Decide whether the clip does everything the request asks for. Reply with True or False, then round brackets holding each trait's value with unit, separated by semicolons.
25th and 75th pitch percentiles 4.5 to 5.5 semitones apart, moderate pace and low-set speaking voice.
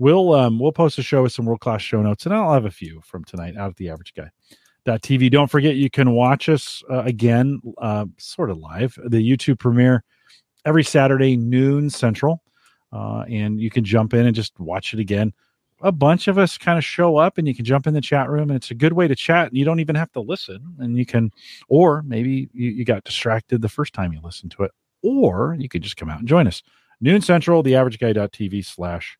False (5.1 semitones; 230 wpm; 125 Hz)